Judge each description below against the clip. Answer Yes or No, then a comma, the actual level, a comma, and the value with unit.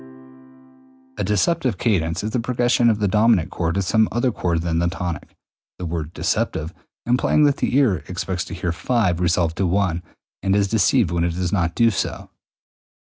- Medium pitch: No, very low, 95 Hz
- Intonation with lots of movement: No, average, 4.9 semitones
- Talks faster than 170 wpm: Yes, average, 180 wpm